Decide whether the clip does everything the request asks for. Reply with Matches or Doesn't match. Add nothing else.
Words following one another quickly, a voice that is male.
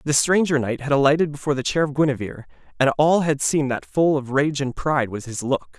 Matches